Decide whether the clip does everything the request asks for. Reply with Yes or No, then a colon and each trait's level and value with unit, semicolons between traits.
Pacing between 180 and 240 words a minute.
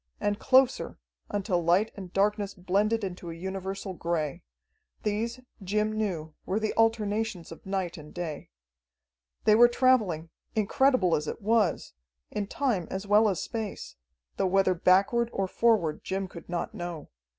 No: average, 150 wpm